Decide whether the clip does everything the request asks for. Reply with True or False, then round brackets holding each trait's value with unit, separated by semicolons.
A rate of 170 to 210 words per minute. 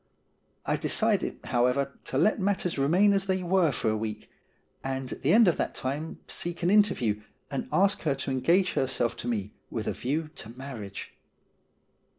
True (175 wpm)